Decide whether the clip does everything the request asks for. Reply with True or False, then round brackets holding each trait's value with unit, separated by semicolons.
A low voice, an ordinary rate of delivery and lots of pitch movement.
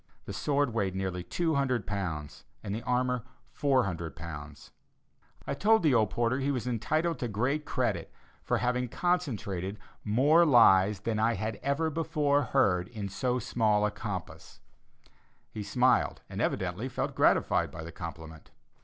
True (115 Hz; 150 wpm; 6.2 semitones)